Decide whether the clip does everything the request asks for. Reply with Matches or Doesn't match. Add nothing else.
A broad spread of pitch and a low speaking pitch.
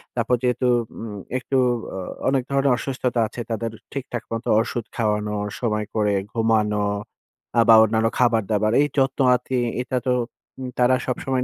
Doesn't match